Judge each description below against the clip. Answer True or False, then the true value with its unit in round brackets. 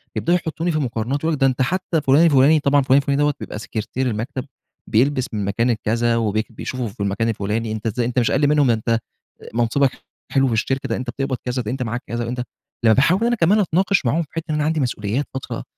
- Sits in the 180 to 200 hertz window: False (130 Hz)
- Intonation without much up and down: False (4.2 semitones)